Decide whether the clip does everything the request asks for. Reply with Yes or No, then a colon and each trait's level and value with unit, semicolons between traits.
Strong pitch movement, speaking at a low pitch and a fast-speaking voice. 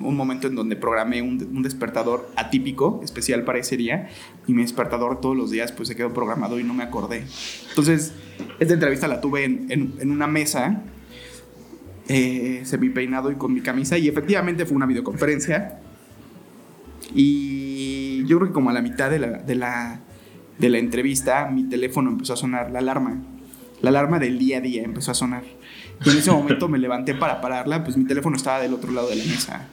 No: narrow, 2.5 semitones; low, 130 Hz; fast, 200 wpm